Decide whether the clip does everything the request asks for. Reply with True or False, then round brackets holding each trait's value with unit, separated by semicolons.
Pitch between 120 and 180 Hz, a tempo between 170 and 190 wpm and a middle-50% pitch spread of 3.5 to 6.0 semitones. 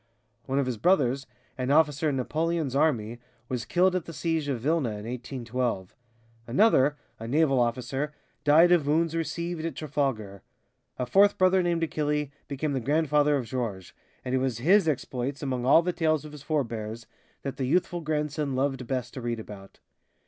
True (140 Hz; 175 wpm; 4.2 semitones)